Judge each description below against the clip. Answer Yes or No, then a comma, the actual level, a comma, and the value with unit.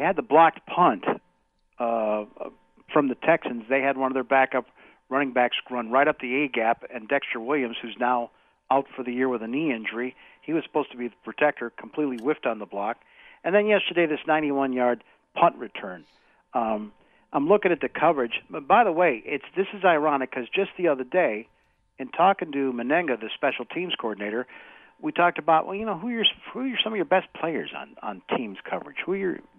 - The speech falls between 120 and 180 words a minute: No, fast, 205 wpm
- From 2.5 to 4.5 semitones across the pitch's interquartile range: No, average, 4.9 semitones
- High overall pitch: No, low, 135 Hz